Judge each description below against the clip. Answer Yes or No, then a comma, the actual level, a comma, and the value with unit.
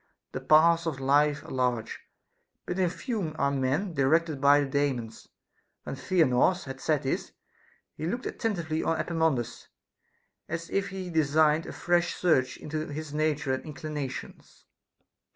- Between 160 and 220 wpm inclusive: No, average, 145 wpm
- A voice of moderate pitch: Yes, medium, 155 Hz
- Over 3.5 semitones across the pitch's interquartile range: No, average, 3.2 semitones